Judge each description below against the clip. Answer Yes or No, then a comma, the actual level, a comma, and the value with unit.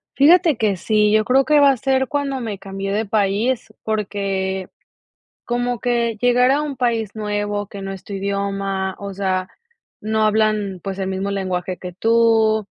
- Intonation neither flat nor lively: Yes, average, 3.6 semitones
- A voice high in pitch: Yes, high, 210 Hz